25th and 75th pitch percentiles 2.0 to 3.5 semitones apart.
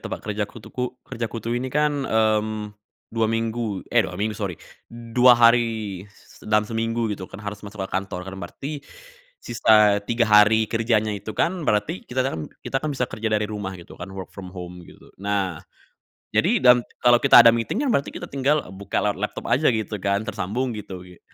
Yes: average, 2.8 semitones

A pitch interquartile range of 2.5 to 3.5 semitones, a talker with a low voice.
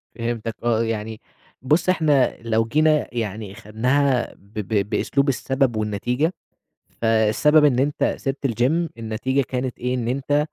No: average, 4.0 semitones; low, 125 Hz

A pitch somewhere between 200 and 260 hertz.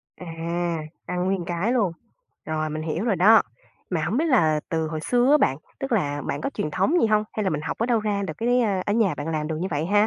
No: high, 190 Hz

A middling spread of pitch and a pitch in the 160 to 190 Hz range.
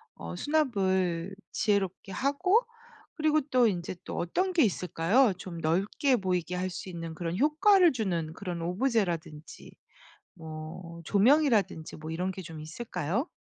No: wide, 7.0 semitones; medium, 185 Hz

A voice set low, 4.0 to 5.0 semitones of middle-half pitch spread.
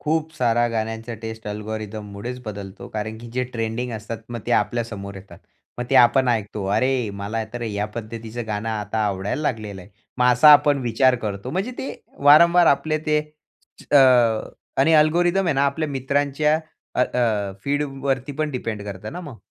Yes: low, 120 Hz; average, 4.4 semitones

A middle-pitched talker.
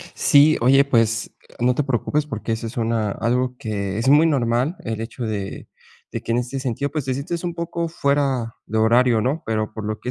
No: low, 125 Hz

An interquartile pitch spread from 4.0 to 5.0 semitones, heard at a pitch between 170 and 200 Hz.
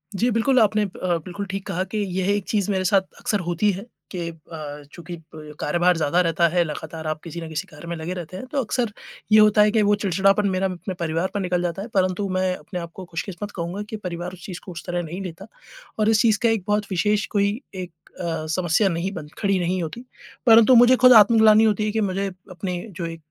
No: average, 3.4 semitones; medium, 185 Hz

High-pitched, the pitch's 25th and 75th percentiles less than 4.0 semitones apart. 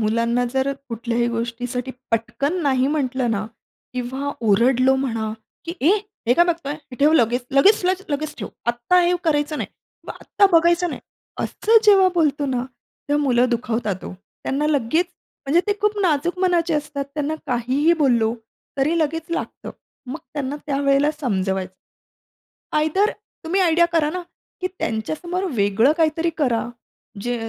No: very high, 280 Hz; average, 5.2 semitones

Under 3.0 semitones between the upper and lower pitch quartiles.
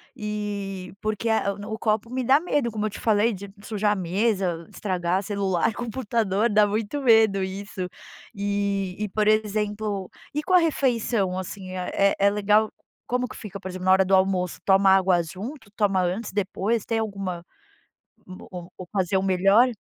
Yes: narrow, 2.5 semitones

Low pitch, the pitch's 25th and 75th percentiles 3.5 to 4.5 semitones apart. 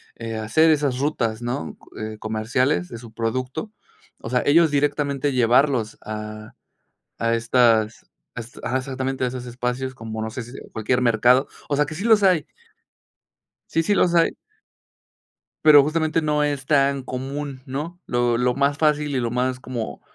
Yes: low, 130 Hz; average, 4.0 semitones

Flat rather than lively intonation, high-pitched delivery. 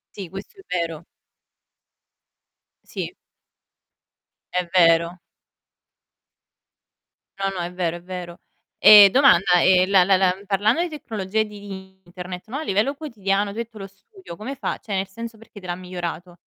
No: average, 3.1 semitones; high, 195 Hz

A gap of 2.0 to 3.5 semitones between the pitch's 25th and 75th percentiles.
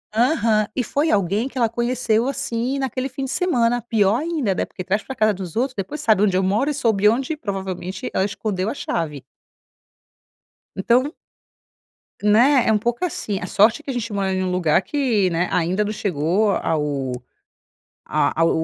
No: average, 5.0 semitones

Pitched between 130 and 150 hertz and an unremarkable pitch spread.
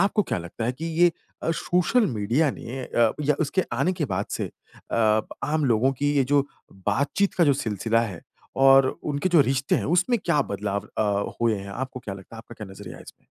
No: low, 135 Hz; wide, 5.9 semitones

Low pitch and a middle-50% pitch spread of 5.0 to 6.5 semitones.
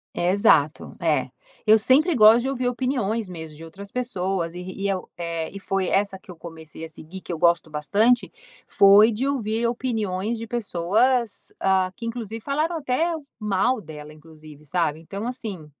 No: high, 200 Hz; wide, 5.6 semitones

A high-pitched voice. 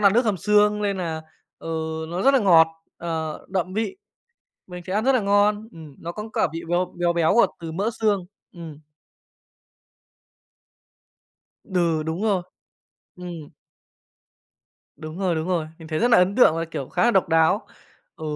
No: medium, 180 Hz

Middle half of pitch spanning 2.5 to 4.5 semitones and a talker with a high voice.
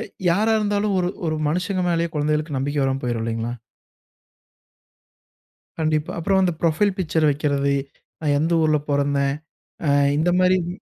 No: average, 4.1 semitones; medium, 155 Hz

